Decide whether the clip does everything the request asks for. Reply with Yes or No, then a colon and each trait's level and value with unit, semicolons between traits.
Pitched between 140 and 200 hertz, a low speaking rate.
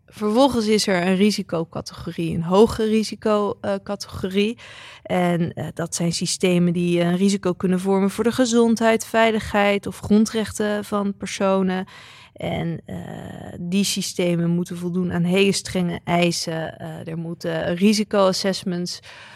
Yes: high, 190 Hz; slow, 125 wpm